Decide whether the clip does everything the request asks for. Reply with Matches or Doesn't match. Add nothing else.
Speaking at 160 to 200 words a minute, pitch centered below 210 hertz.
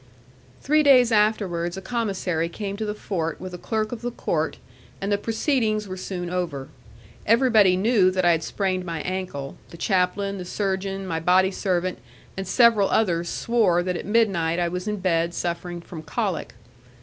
Matches